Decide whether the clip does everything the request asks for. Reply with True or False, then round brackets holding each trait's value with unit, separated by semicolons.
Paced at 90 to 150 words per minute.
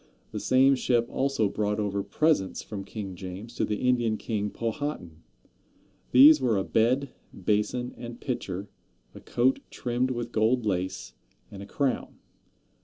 True (145 wpm)